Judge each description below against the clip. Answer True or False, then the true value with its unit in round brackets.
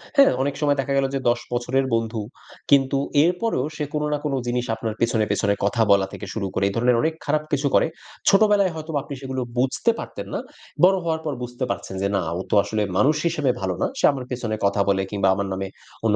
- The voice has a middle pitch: False (130 Hz)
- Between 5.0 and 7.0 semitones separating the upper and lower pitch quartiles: True (5.6 semitones)